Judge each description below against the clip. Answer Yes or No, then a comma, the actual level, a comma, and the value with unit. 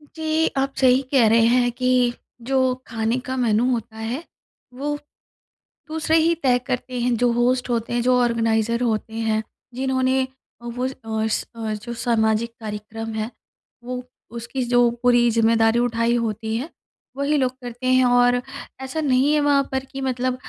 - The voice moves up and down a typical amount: No, narrow, 2.2 semitones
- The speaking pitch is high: Yes, high, 245 Hz